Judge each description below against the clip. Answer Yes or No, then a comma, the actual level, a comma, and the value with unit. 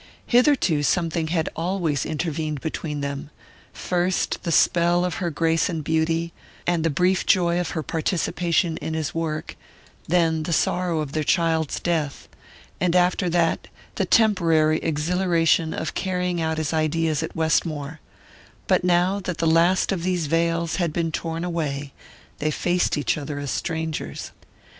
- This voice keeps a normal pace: Yes, average, 150 wpm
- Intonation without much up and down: Yes, narrow, 1.9 semitones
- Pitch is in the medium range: Yes, medium, 165 Hz